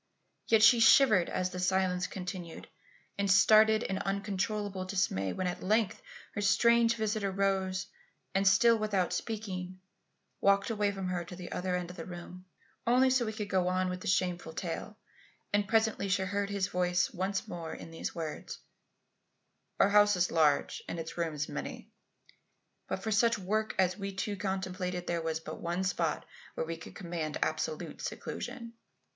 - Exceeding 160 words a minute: Yes, average, 170 wpm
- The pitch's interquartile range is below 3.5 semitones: Yes, narrow, 2.6 semitones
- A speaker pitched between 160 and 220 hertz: Yes, high, 190 Hz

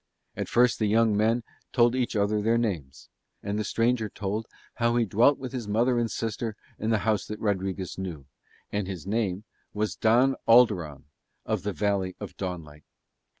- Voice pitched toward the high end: No, low, 105 Hz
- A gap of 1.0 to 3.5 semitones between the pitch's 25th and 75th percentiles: Yes, average, 3.2 semitones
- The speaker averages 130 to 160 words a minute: No, average, 175 wpm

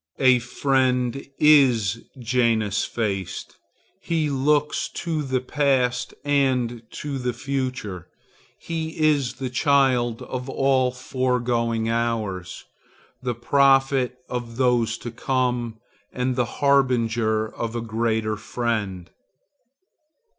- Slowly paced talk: Yes, slow, 105 wpm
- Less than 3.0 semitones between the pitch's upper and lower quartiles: Yes, narrow, 2.6 semitones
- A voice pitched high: No, low, 125 Hz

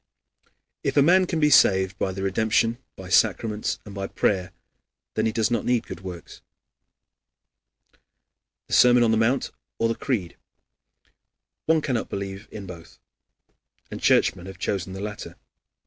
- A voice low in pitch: Yes, low, 105 Hz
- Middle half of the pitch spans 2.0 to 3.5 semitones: No, average, 3.9 semitones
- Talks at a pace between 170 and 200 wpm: No, average, 150 wpm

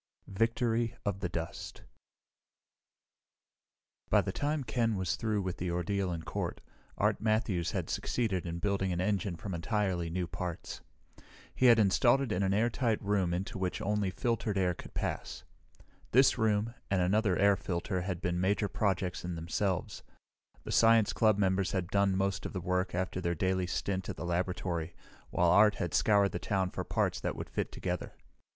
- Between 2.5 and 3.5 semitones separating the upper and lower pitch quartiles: Yes, average, 2.9 semitones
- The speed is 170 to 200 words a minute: Yes, average, 175 wpm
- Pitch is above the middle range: No, very low, 95 Hz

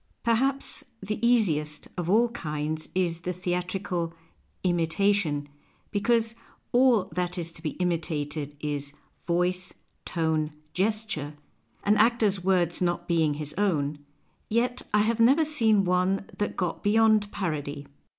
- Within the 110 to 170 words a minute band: Yes, slow, 135 wpm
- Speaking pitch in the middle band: Yes, medium, 180 Hz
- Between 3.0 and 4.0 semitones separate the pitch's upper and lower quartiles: No, average, 5.1 semitones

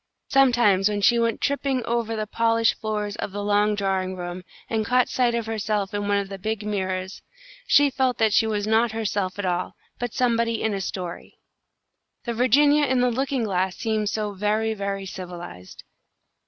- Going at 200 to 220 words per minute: No, average, 180 wpm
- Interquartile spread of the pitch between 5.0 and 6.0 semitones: No, average, 2.9 semitones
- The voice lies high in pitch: Yes, high, 215 Hz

